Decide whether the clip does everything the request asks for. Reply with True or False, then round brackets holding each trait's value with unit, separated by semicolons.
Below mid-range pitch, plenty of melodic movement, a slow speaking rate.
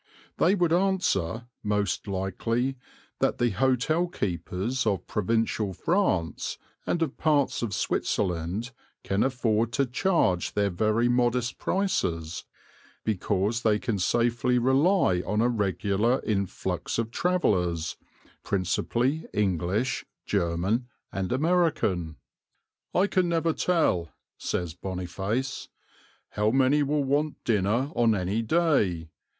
True (115 Hz; 5.9 semitones; 110 wpm)